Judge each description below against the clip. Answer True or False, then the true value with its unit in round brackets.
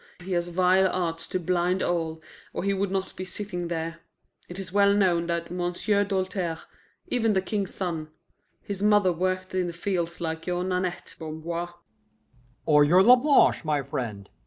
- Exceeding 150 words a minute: True (170 wpm)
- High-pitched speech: False (180 Hz)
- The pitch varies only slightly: True (2.3 semitones)